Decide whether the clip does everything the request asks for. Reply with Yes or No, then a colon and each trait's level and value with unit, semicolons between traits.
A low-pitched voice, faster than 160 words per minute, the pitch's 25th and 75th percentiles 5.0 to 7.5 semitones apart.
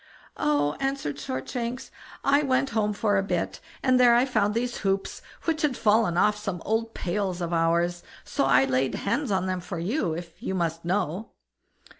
No: high, 200 Hz; average, 180 wpm; wide, 5.6 semitones